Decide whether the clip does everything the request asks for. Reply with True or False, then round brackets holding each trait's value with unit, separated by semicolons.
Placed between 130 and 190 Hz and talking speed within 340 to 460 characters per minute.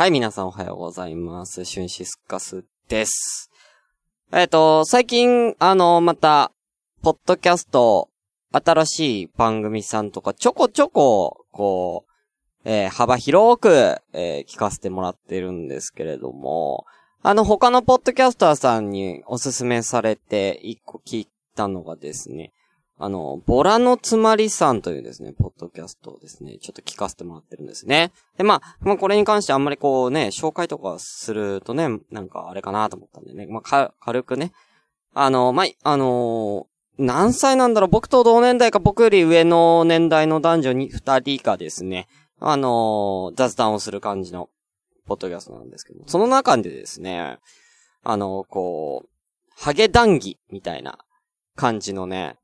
False (135 Hz; 320 characters per minute)